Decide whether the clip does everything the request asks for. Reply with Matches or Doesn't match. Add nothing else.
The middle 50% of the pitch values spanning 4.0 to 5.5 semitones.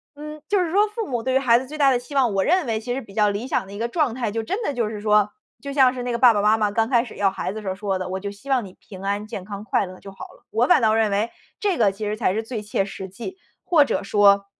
Matches